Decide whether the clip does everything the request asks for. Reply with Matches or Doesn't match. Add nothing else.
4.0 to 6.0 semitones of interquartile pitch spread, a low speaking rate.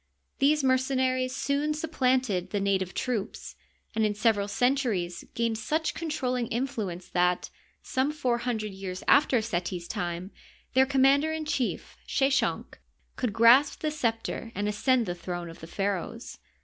Doesn't match